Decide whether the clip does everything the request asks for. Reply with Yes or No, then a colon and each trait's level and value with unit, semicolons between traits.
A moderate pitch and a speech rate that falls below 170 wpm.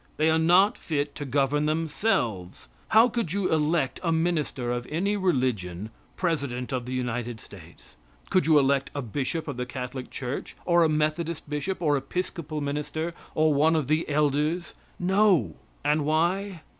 Yes: medium, 150 Hz; average, 160 wpm